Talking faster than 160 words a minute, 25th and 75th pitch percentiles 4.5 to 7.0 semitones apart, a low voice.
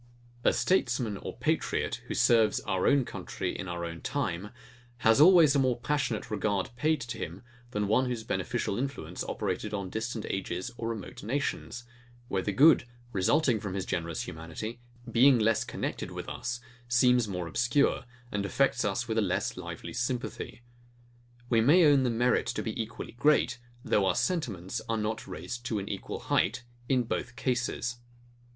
No: average, 170 wpm; average, 3.8 semitones; low, 115 Hz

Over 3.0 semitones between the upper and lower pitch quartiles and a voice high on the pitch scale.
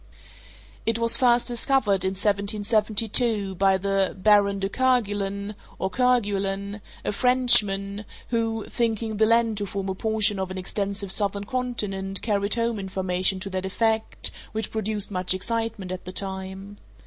No: narrow, 2.6 semitones; high, 205 Hz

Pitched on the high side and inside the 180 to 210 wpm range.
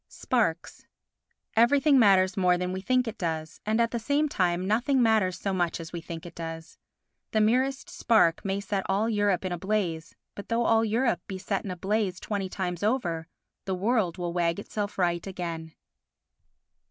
Yes: high, 195 Hz; average, 185 wpm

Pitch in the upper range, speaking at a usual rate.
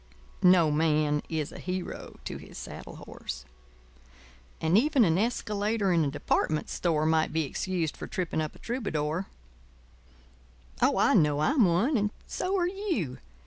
No: medium, 175 Hz; average, 150 wpm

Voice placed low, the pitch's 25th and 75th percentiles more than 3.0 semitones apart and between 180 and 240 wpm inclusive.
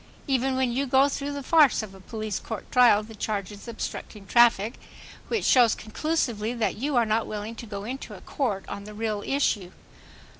No: high, 230 Hz; average, 3.9 semitones; average, 190 wpm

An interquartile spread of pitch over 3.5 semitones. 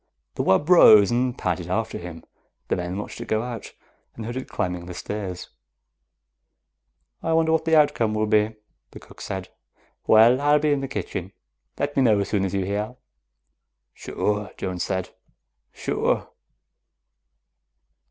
Yes: wide, 5.4 semitones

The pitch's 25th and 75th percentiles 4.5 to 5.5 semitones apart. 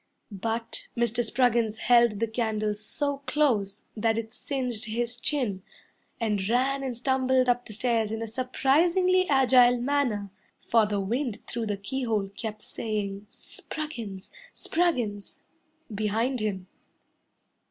No: average, 3.3 semitones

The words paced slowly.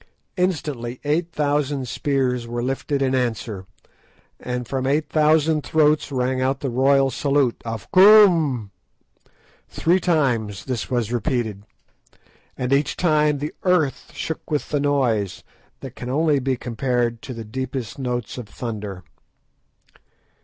Yes: slow, 130 wpm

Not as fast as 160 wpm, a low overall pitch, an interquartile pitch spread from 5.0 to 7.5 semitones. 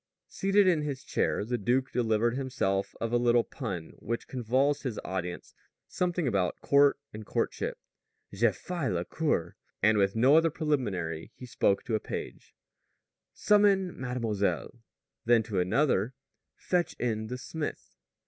Yes: average, 145 wpm; low, 120 Hz; wide, 5.5 semitones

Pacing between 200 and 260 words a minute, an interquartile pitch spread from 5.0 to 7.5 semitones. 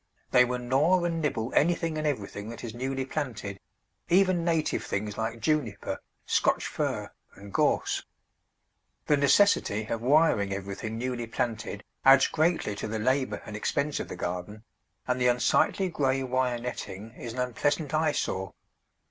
No: average, 150 wpm; wide, 5.4 semitones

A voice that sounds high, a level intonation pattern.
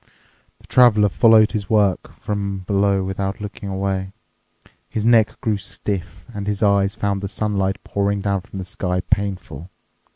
No: low, 100 Hz; narrow, 1.4 semitones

